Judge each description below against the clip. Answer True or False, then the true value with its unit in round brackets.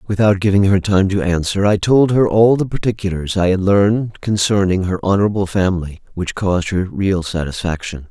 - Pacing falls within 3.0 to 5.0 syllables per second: False (5.4 syllables/s)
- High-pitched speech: False (95 Hz)